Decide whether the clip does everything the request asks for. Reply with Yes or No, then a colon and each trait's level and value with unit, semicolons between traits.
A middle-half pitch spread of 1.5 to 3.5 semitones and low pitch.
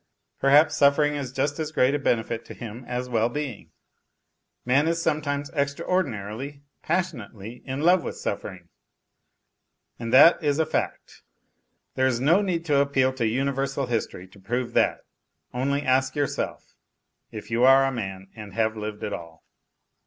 No: average, 4.0 semitones; low, 130 Hz